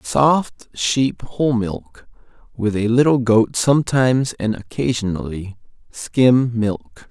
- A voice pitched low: Yes, low, 115 Hz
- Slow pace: Yes, slow, 110 wpm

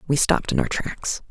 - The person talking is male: No, female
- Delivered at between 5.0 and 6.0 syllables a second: Yes, 5.5 syllables/s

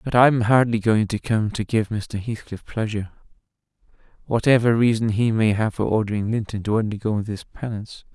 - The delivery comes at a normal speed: Yes, average, 170 wpm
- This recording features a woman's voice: No, male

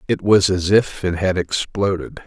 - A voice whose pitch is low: Yes, very low, 95 Hz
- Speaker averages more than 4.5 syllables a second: No, 4.3 syllables/s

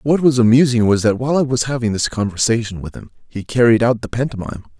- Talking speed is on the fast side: Yes, fast, 225 wpm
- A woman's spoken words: No, male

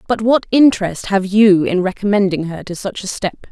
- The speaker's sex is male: No, female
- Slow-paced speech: No, fast, 205 wpm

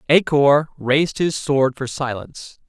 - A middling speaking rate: Yes, average, 155 wpm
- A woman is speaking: No, male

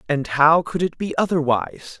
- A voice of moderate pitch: Yes, medium, 155 Hz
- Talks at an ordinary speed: Yes, average, 180 wpm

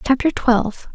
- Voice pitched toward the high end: Yes, very high, 250 Hz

